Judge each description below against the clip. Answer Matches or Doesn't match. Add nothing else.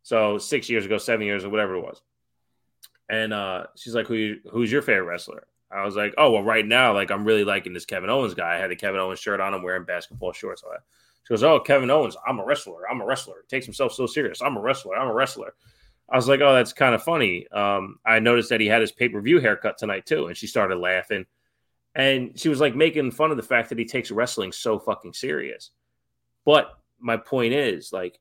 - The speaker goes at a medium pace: Doesn't match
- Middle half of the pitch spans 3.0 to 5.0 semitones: Matches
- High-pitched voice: Doesn't match